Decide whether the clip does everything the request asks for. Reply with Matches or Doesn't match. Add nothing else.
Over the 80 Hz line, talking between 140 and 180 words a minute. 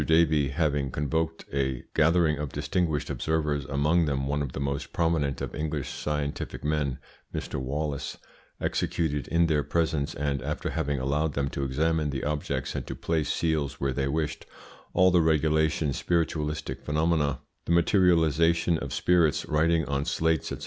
Doesn't match